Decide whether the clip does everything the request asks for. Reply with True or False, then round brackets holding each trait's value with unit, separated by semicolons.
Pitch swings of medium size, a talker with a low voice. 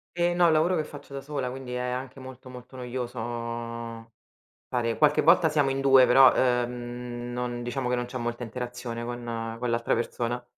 False (1.9 semitones; 125 Hz)